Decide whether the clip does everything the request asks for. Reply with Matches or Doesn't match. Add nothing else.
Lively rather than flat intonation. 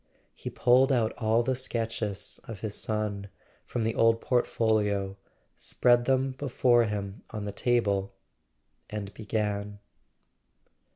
Doesn't match